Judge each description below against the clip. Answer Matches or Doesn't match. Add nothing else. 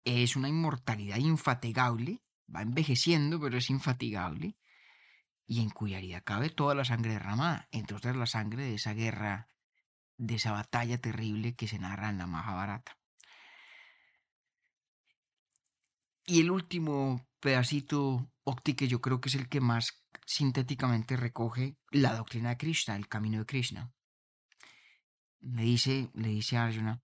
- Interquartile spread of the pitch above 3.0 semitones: Matches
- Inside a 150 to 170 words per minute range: Doesn't match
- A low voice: Matches